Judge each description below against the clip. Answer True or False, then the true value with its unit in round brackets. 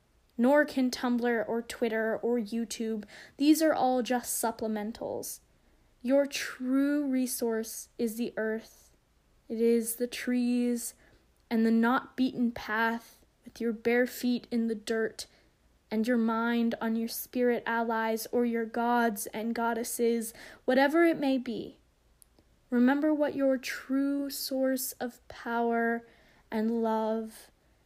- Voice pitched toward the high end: True (235 Hz)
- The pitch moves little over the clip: True (2.1 semitones)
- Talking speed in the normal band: False (125 wpm)